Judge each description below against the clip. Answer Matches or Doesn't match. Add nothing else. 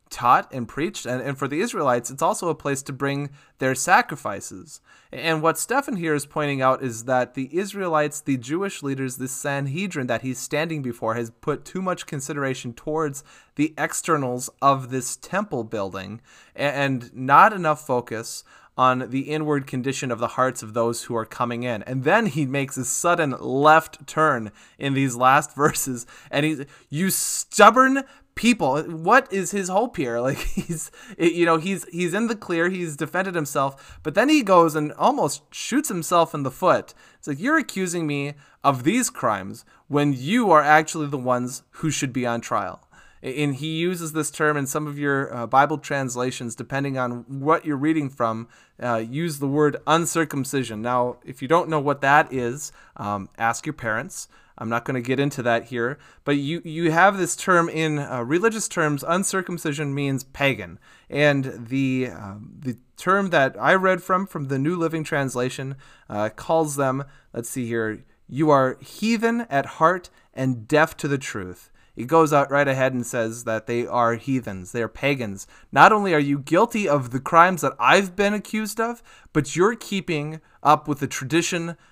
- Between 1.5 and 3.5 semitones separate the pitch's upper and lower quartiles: Doesn't match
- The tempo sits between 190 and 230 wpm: Doesn't match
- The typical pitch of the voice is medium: Matches